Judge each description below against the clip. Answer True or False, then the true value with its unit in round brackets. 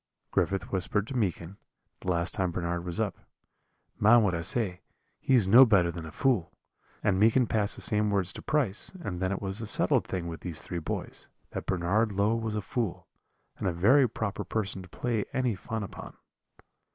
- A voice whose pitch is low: True (100 Hz)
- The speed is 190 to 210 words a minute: True (200 wpm)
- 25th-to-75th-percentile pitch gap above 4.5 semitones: False (3.8 semitones)